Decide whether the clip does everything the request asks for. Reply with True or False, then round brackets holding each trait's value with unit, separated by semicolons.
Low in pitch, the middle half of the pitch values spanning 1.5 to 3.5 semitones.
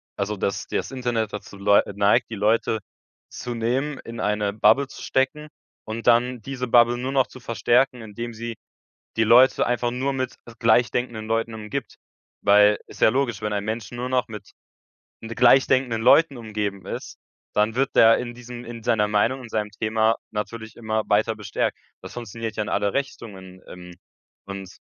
True (115 Hz; 2.6 semitones)